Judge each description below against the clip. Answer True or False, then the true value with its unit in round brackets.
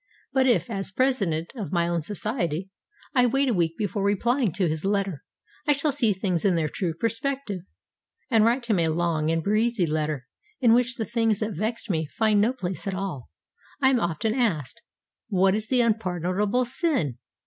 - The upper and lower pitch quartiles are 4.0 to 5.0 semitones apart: False (5.5 semitones)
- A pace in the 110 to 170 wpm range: False (185 wpm)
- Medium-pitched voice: False (205 Hz)